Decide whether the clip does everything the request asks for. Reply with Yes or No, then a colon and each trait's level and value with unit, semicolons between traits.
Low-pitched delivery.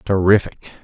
Yes: very low, 95 Hz